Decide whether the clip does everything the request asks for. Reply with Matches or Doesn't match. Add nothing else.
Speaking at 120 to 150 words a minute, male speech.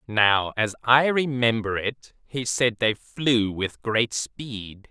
Matches